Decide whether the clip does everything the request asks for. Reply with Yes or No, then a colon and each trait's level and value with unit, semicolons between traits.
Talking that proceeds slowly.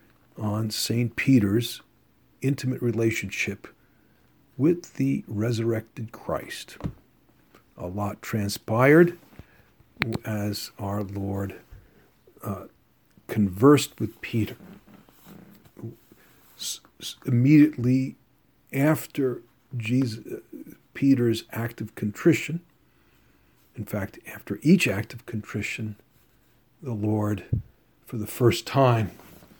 Yes: slow, 80 wpm